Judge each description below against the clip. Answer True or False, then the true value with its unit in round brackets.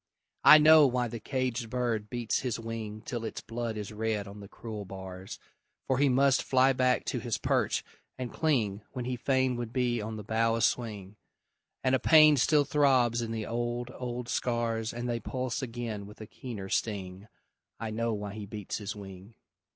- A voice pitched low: True (115 Hz)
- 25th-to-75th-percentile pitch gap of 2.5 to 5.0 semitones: True (2.9 semitones)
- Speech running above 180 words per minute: True (190 wpm)